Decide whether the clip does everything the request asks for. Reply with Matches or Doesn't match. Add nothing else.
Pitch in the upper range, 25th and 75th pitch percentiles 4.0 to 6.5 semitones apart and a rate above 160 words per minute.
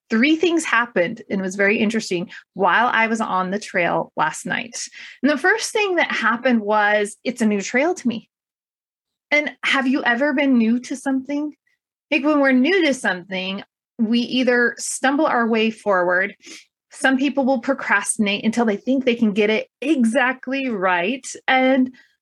Matches